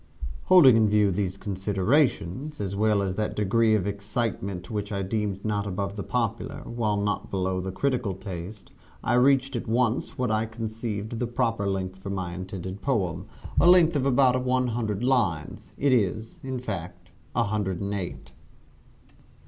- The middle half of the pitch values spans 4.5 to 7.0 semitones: No, average, 4.0 semitones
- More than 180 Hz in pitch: No, low, 105 Hz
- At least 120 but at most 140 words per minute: No, average, 165 wpm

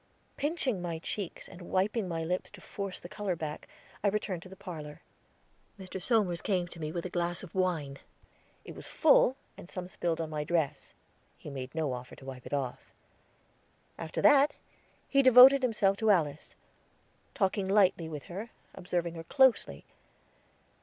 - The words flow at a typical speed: Yes, average, 165 wpm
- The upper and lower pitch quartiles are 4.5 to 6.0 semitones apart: No, average, 4.1 semitones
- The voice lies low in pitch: No, medium, 180 Hz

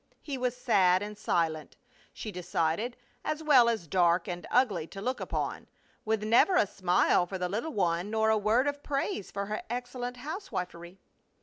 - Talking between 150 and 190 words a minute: Yes, average, 175 wpm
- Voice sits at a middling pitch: No, high, 210 Hz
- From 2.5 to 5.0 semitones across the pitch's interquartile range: No, wide, 5.6 semitones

